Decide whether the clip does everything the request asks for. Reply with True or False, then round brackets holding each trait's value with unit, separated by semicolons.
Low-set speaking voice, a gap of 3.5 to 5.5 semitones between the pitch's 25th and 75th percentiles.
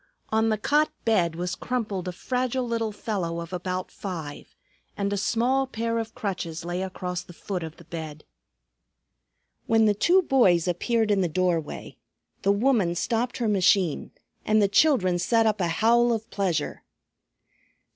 False (200 Hz; 4.5 semitones)